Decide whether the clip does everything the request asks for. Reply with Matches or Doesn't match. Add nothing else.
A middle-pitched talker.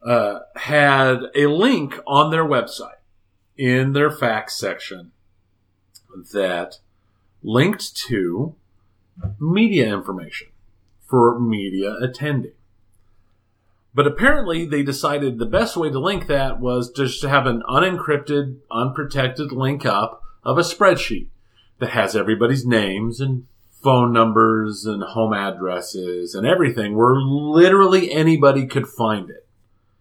Doesn't match